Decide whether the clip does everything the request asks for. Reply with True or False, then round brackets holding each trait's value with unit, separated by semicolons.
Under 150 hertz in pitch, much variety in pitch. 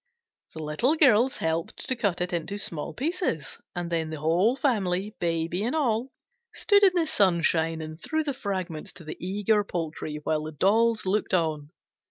False (185 Hz; 6.3 semitones)